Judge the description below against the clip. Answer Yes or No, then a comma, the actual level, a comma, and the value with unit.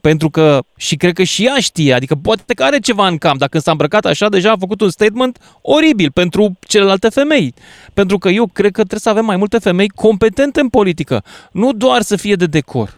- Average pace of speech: No, fast, 220 wpm